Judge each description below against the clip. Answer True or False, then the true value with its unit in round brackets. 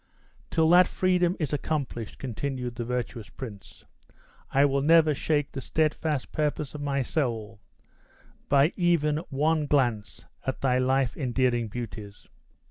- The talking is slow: True (130 wpm)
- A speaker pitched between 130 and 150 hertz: True (140 Hz)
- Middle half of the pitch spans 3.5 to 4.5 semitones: True (3.9 semitones)